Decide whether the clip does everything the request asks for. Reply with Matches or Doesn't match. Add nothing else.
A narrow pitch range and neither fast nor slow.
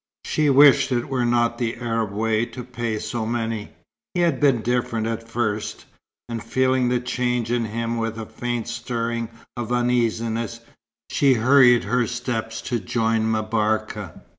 Matches